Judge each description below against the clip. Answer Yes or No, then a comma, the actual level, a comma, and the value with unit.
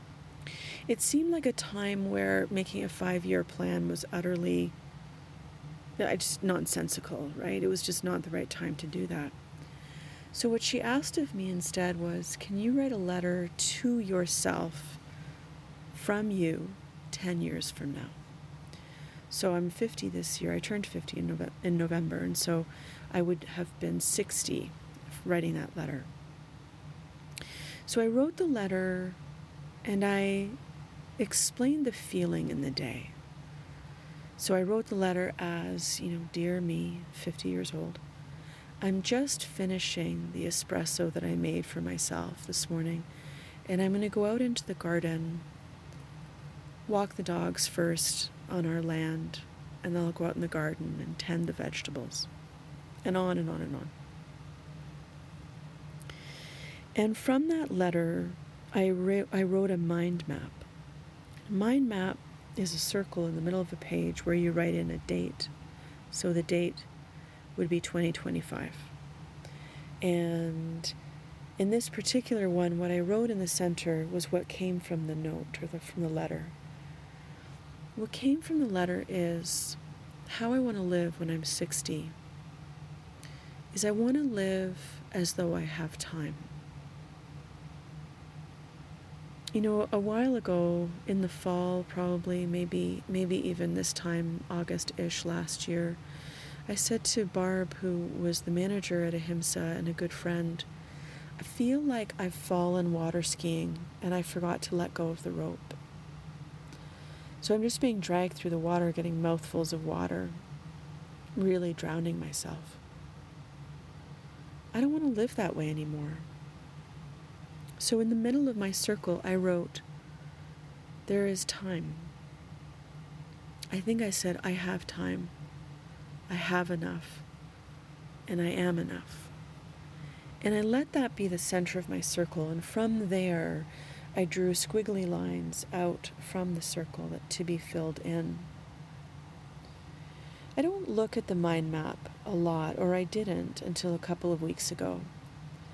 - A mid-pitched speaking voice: Yes, medium, 165 Hz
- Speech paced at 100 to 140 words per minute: No, average, 150 wpm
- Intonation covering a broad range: No, average, 3.4 semitones